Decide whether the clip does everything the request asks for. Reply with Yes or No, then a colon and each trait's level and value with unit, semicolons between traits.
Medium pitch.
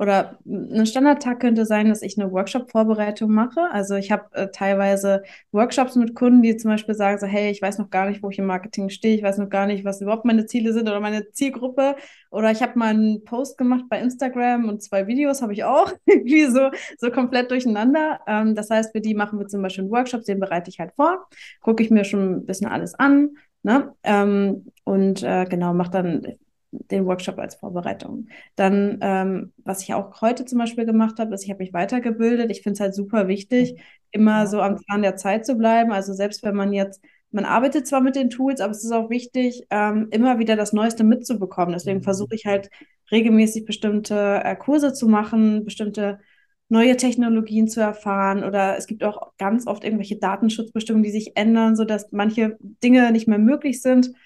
No: high, 215 Hz